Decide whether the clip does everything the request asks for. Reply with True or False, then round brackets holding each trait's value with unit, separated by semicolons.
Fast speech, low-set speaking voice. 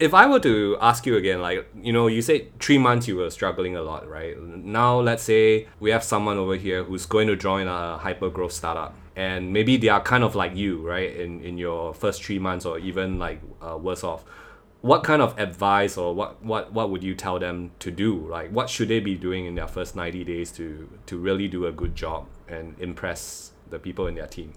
True (235 wpm; 95 Hz)